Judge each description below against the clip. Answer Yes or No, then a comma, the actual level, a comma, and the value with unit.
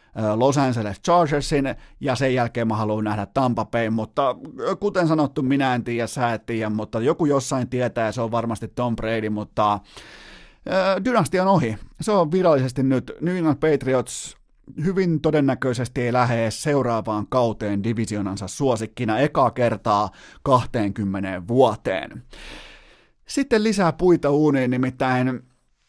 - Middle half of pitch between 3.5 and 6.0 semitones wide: Yes, average, 4.6 semitones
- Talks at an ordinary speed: Yes, average, 135 wpm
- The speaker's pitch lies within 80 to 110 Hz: No, low, 125 Hz